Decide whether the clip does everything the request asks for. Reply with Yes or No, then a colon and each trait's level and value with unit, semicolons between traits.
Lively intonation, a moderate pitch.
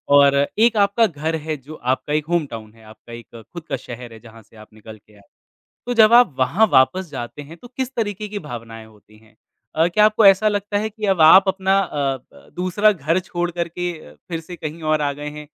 Yes: wide, 8.6 semitones; medium, 160 Hz